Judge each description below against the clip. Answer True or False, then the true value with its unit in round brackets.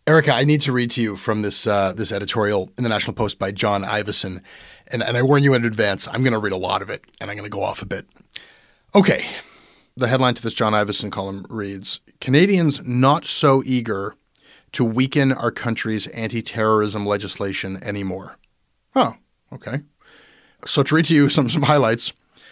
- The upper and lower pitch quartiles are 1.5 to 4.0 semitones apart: False (4.5 semitones)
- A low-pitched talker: True (115 Hz)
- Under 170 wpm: False (195 wpm)